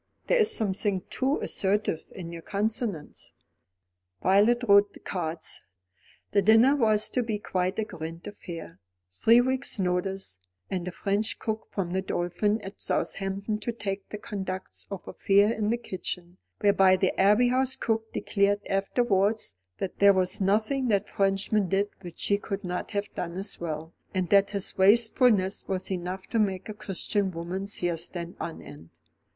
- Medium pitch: No, high, 195 Hz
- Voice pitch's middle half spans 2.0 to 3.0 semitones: Yes, average, 2.7 semitones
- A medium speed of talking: Yes, average, 160 wpm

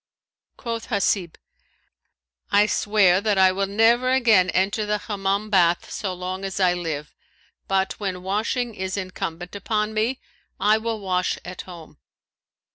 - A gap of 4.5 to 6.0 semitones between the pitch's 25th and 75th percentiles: No, average, 2.7 semitones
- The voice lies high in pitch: Yes, high, 195 Hz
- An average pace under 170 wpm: Yes, average, 140 wpm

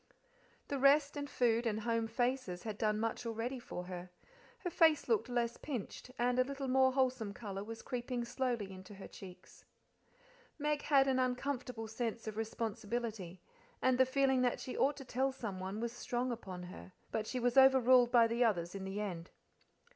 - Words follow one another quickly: No, average, 180 wpm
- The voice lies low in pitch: No, high, 240 Hz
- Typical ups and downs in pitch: Yes, average, 3.5 semitones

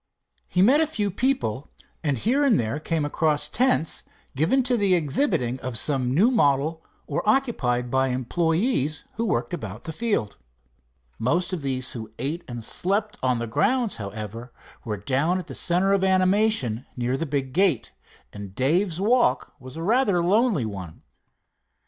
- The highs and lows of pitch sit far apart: Yes, wide, 8.2 semitones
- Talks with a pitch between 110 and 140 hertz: No, medium, 155 Hz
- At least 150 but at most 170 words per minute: Yes, average, 160 wpm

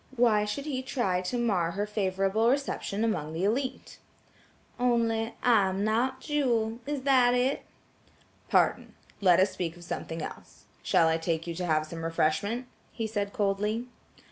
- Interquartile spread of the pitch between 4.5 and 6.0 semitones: Yes, average, 5.2 semitones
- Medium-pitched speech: No, high, 210 Hz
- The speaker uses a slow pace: No, average, 160 wpm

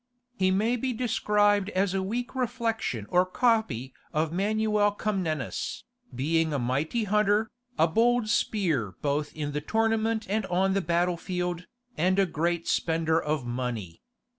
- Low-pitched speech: No, medium, 185 Hz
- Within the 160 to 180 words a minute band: No, average, 145 wpm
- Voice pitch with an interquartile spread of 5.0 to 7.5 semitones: Yes, wide, 5.4 semitones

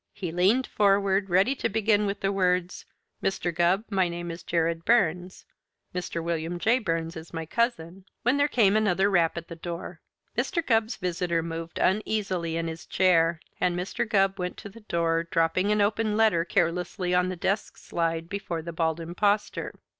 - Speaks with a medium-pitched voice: Yes, medium, 180 Hz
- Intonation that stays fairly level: No, average, 3.3 semitones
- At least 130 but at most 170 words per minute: No, average, 180 wpm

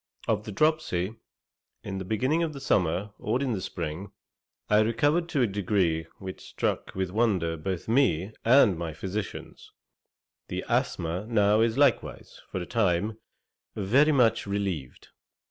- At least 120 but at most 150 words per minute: Yes, average, 145 wpm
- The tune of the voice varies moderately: Yes, average, 4.3 semitones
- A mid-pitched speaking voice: No, low, 105 Hz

